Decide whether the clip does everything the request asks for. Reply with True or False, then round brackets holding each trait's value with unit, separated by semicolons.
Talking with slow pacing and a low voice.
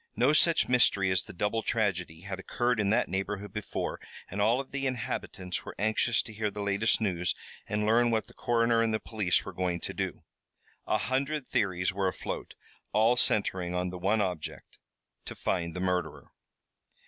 False (185 wpm; 105 Hz)